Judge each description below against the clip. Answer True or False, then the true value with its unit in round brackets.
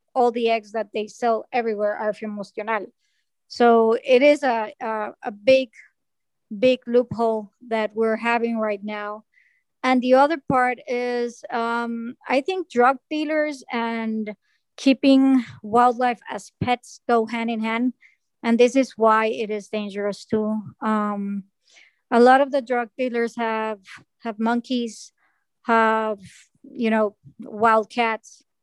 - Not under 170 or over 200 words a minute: False (135 wpm)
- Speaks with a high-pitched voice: True (235 Hz)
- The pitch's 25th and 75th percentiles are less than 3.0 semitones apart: True (2.5 semitones)